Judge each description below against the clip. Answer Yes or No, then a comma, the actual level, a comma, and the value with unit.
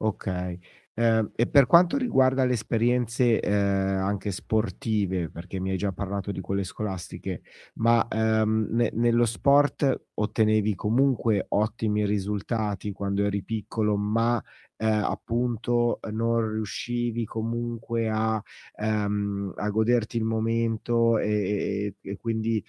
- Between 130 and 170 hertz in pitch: No, low, 110 Hz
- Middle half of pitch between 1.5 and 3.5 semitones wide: Yes, narrow, 2.4 semitones